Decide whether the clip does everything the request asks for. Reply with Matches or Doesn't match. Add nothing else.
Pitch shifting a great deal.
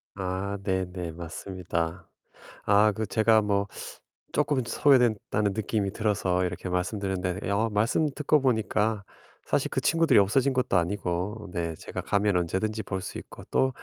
Doesn't match